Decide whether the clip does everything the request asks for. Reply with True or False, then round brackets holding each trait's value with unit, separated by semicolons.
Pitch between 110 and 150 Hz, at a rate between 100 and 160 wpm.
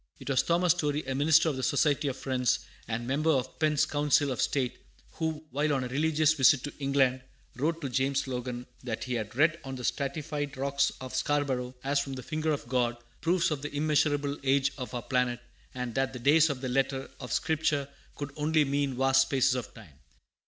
False (140 Hz; 205 wpm)